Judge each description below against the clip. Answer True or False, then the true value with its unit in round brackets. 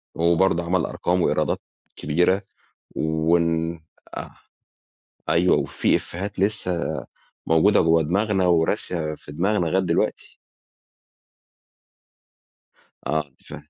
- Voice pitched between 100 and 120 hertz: False (85 Hz)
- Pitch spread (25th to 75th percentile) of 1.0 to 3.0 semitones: True (2.6 semitones)